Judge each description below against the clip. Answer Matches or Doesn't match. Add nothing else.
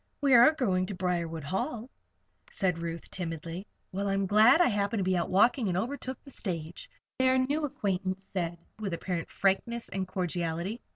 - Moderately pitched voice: Doesn't match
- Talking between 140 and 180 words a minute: Matches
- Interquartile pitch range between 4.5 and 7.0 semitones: Matches